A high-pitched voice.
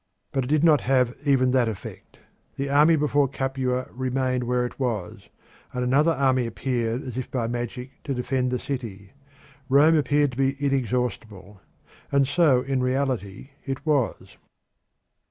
No: low, 130 Hz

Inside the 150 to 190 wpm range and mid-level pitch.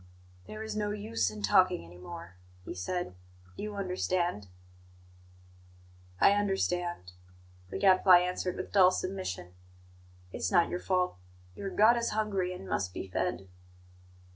No: slow, 135 wpm; medium, 180 Hz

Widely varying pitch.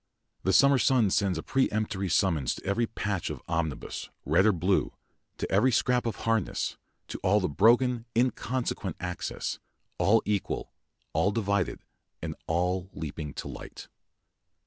No: average, 4.2 semitones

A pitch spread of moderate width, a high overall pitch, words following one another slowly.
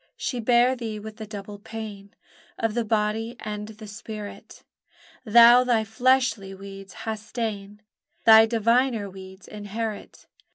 No: narrow, 2.0 semitones; high, 220 Hz; slow, 130 wpm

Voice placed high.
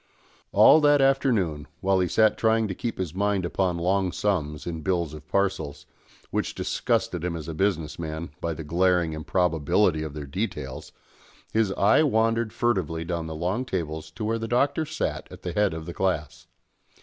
No: very low, 90 Hz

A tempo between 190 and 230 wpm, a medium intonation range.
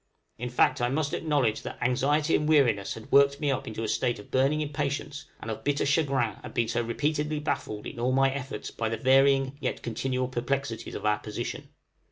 Yes: fast, 205 wpm; average, 3.5 semitones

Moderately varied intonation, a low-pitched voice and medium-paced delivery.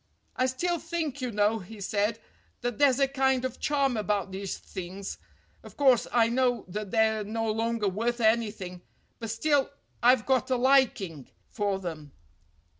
No: average, 4.1 semitones; high, 225 Hz; average, 160 wpm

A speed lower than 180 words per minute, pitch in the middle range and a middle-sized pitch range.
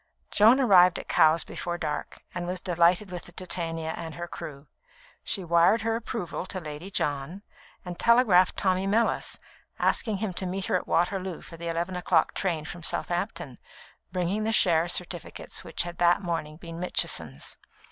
No: average, 165 wpm; medium, 175 Hz; narrow, 2.3 semitones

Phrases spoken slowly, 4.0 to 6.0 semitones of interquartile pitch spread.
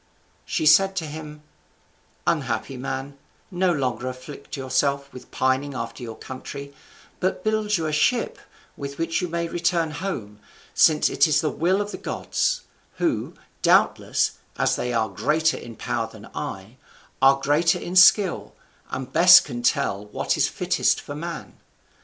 No: average, 155 wpm; average, 4.6 semitones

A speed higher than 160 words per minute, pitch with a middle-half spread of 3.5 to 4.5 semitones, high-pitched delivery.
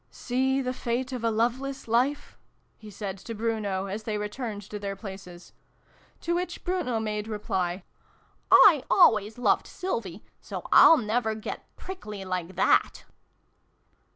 No: average, 145 wpm; average, 4.0 semitones; high, 220 Hz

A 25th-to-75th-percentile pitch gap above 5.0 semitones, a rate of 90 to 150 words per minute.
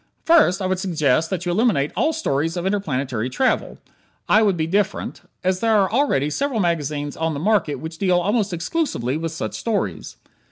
No: wide, 5.4 semitones; average, 185 wpm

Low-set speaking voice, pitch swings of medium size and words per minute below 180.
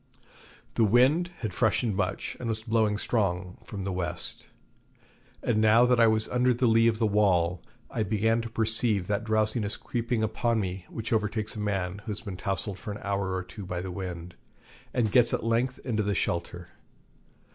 No: low, 110 Hz; average, 3.0 semitones; average, 185 wpm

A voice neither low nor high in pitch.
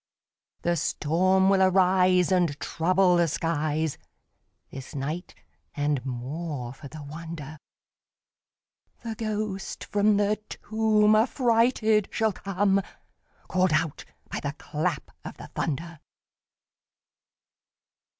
Yes: medium, 180 Hz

